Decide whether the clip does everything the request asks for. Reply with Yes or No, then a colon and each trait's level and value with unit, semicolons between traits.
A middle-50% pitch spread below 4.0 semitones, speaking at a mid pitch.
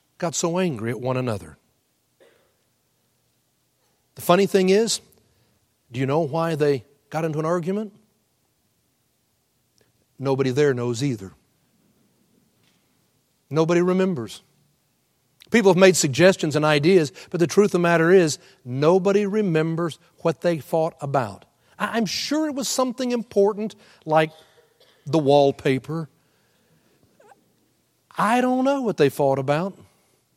No: wide, 5.5 semitones; medium, 160 Hz